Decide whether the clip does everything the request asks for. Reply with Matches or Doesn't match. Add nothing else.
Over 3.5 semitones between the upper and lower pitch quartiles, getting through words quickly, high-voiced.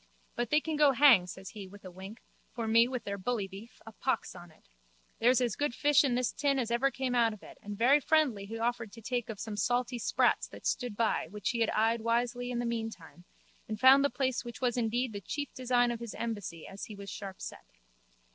Doesn't match